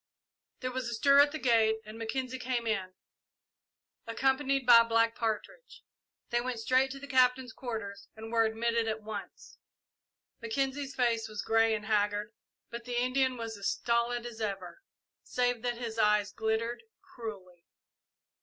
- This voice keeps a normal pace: Yes, average, 155 wpm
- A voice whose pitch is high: Yes, high, 230 Hz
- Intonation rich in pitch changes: No, narrow, 2.4 semitones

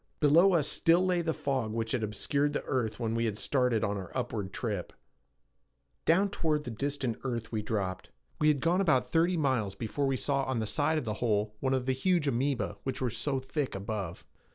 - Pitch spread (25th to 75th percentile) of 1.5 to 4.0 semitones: No, average, 5.1 semitones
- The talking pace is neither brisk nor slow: No, fast, 210 wpm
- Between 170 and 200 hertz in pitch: No, low, 130 Hz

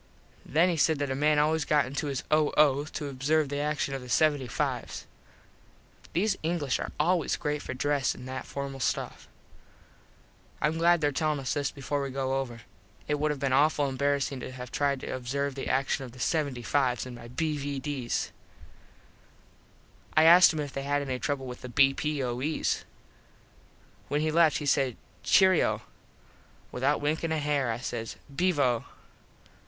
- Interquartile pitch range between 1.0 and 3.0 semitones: Yes, narrow, 2.5 semitones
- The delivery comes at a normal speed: Yes, average, 165 wpm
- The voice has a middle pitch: Yes, medium, 145 Hz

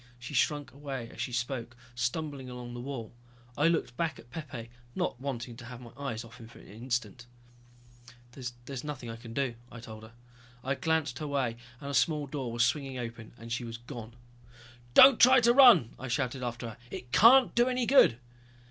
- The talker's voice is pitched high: No, low, 125 Hz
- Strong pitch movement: No, average, 3.6 semitones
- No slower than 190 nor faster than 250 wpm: Yes, average, 200 wpm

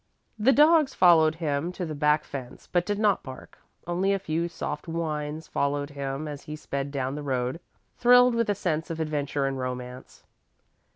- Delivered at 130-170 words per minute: No, average, 180 wpm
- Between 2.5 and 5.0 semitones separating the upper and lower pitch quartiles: Yes, average, 4.0 semitones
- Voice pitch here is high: No, medium, 155 Hz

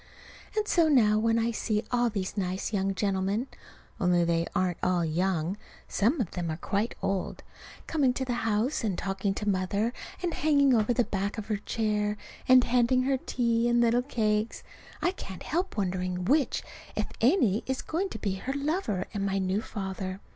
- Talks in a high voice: Yes, high, 215 Hz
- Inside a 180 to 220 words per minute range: Yes, average, 185 wpm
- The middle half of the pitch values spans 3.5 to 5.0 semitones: Yes, average, 4.4 semitones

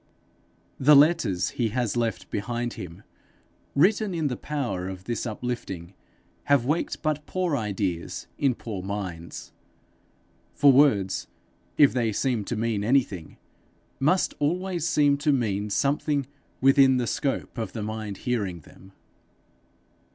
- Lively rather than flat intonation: Yes, wide, 5.9 semitones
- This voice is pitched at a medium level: No, low, 120 Hz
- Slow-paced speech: Yes, slow, 130 wpm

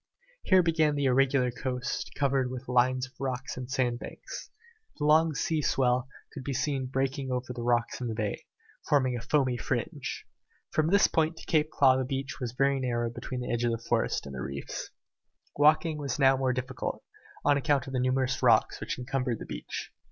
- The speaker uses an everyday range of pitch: No, narrow, 2.2 semitones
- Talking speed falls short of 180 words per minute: No, average, 195 wpm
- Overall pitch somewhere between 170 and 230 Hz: No, low, 130 Hz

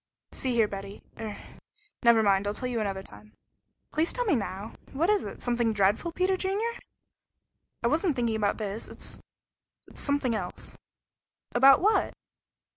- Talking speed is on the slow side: No, average, 160 wpm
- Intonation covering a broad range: Yes, wide, 7.6 semitones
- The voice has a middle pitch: No, high, 235 Hz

